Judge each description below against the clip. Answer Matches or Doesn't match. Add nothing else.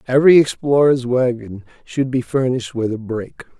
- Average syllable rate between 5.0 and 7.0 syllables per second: Matches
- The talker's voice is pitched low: Matches